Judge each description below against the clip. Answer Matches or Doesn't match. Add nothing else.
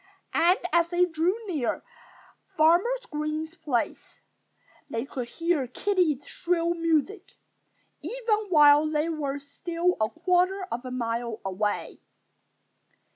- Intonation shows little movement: Doesn't match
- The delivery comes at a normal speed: Doesn't match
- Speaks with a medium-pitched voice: Doesn't match